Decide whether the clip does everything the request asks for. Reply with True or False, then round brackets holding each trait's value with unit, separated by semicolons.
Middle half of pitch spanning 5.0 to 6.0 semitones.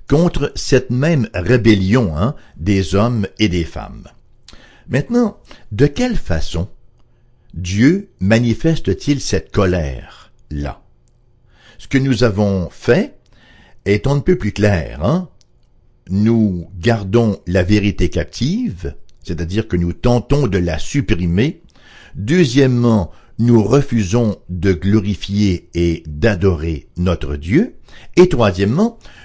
True (5.3 semitones)